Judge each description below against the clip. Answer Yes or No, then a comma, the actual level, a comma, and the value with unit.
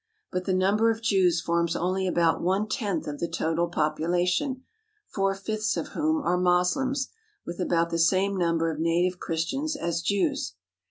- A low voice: No, medium, 180 Hz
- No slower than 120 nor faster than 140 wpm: No, average, 165 wpm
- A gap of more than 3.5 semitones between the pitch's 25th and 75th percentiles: No, average, 3.2 semitones